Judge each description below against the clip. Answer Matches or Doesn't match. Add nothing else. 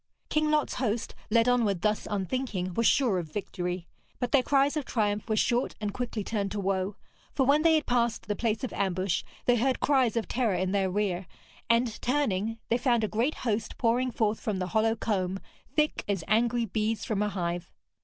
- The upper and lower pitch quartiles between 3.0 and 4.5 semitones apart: Matches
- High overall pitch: Matches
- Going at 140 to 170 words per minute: Doesn't match